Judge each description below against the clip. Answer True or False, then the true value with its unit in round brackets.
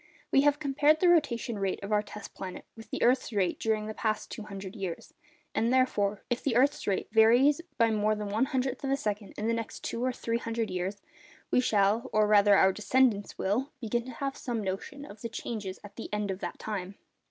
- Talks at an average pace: False (210 wpm)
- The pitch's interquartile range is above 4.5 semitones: False (3.8 semitones)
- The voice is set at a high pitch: True (220 Hz)